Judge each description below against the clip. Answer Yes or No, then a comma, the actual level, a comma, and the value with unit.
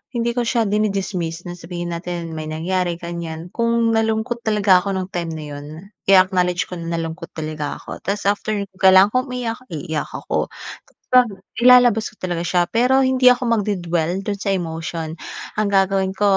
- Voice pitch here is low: No, high, 190 Hz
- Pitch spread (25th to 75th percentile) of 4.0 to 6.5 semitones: Yes, average, 4.4 semitones